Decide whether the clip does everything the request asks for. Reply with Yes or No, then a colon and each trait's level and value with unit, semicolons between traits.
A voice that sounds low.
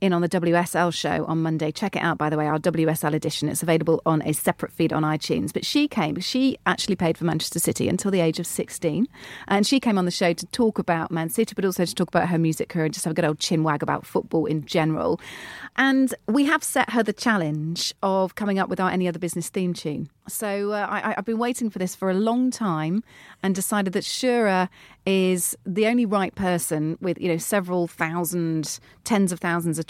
No: medium, 180 Hz